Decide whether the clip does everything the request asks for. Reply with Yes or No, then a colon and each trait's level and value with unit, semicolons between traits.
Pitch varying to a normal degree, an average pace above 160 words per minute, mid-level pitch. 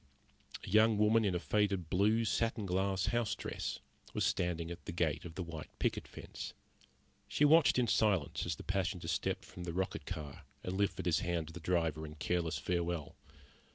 No: average, 3.8 semitones; average, 190 wpm; very low, 90 Hz